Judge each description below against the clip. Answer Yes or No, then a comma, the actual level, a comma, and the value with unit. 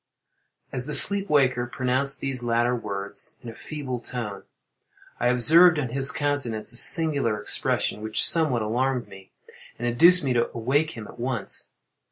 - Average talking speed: Yes, average, 160 wpm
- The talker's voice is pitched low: Yes, low, 125 Hz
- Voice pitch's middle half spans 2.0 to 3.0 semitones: No, average, 3.7 semitones